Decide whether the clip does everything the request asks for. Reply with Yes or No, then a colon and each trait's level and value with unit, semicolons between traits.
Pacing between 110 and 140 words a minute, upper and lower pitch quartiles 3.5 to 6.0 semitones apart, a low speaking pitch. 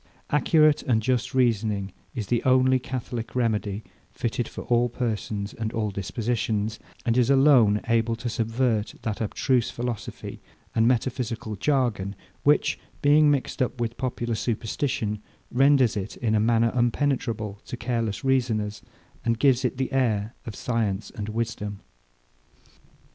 No: slow, 135 wpm; average, 2.8 semitones; low, 115 Hz